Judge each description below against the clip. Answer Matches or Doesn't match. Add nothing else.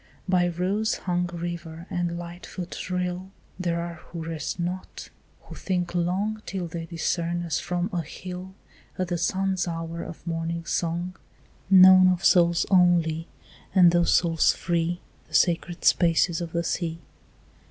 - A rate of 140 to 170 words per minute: Matches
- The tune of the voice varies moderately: Doesn't match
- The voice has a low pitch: Doesn't match